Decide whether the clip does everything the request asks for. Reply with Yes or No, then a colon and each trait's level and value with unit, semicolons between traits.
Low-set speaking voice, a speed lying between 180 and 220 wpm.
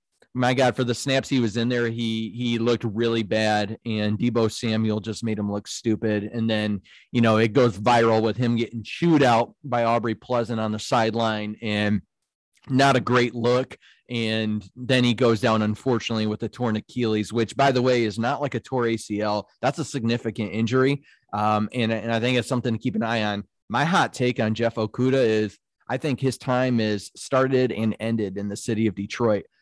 Yes: low, 115 Hz; fast, 205 wpm